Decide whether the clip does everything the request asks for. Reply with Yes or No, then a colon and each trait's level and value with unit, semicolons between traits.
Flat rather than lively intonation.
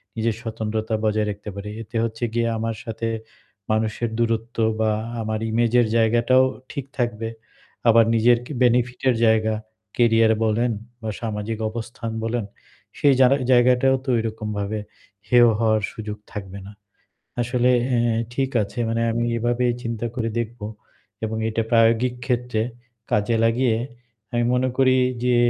Yes: narrow, 1.7 semitones